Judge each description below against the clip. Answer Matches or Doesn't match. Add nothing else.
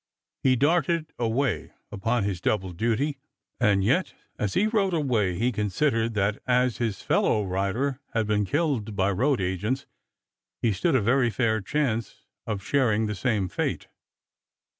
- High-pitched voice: Doesn't match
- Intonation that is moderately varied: Matches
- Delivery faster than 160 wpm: Doesn't match